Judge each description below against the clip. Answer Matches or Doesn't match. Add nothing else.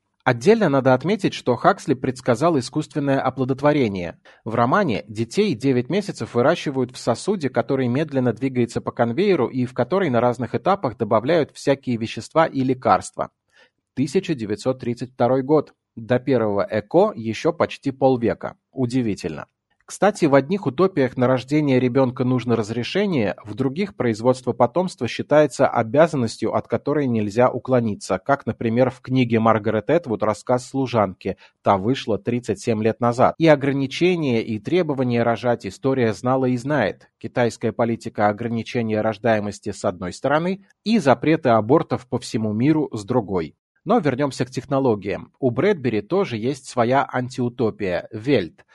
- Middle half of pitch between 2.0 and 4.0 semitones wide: Matches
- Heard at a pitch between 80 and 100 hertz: Doesn't match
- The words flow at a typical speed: Matches